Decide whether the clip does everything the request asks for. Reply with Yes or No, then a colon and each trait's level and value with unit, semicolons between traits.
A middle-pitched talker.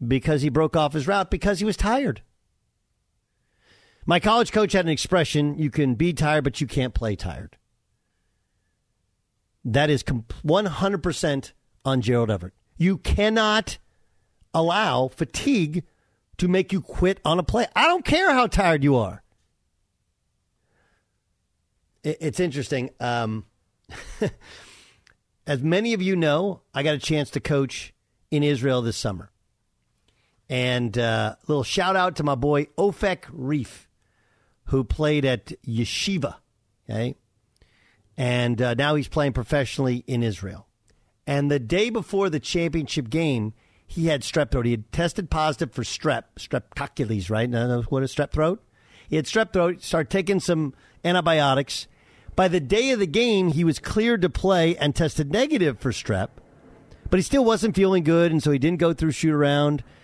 Yes: medium, 145 Hz